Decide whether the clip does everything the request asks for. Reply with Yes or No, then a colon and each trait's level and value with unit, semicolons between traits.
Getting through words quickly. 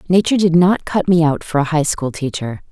Yes: fast, 220 wpm